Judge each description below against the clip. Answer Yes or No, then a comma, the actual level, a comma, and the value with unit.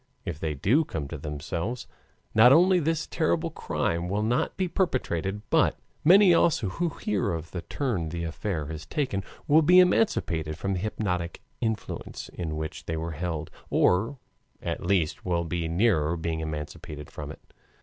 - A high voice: No, very low, 90 Hz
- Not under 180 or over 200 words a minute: No, average, 165 wpm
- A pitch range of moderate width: No, wide, 8.1 semitones